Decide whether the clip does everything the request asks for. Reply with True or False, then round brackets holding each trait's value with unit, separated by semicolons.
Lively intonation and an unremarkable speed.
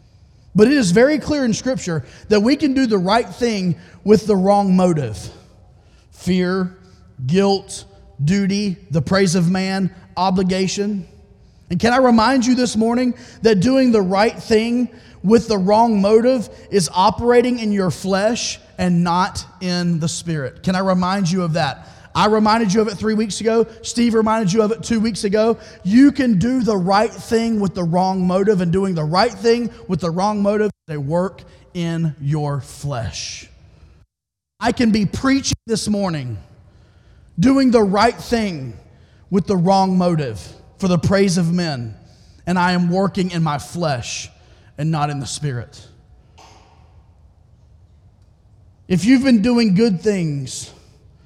True (6.4 semitones; 160 wpm)